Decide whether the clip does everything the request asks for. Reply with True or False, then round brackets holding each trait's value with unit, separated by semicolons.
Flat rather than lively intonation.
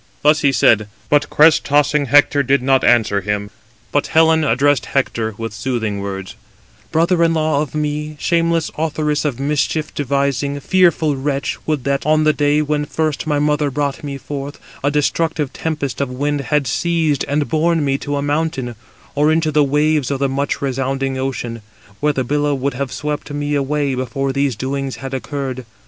True (2.1 semitones)